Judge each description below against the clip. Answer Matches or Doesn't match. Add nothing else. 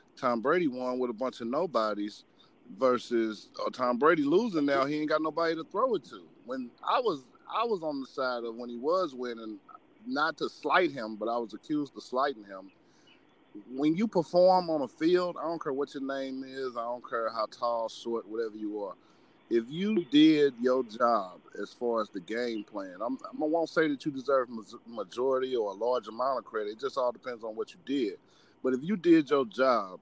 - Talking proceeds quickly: Matches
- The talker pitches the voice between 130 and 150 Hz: Matches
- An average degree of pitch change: Doesn't match